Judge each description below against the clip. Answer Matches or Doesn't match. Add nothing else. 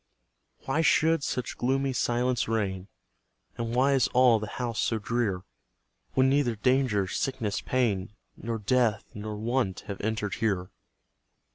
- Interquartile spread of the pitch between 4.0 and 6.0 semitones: Doesn't match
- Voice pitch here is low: Matches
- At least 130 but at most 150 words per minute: Matches